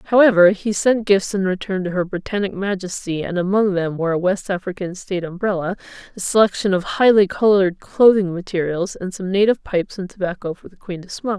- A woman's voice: Yes, female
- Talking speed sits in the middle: Yes, average, 195 wpm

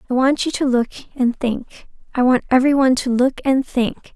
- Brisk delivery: Yes, fast, 215 wpm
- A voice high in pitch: Yes, very high, 255 Hz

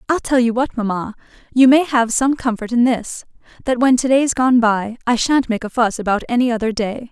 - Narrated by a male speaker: No, female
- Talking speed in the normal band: No, fast, 220 wpm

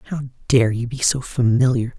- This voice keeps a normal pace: Yes, average, 180 wpm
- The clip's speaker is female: No, male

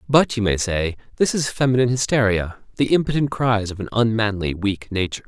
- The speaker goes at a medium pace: Yes, average, 180 wpm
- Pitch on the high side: No, low, 110 Hz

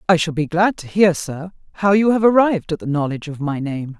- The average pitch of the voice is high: No, medium, 170 Hz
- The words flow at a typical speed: No, fast, 255 wpm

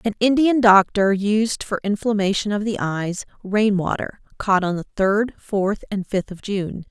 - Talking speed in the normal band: Yes, average, 175 wpm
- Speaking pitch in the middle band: No, high, 205 Hz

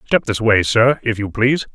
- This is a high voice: No, low, 115 Hz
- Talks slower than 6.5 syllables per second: Yes, 5.3 syllables/s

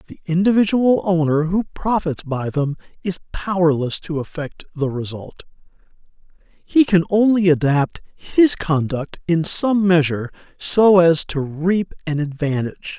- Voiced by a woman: No, male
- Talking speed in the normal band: No, slow, 130 wpm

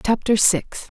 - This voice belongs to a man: No, female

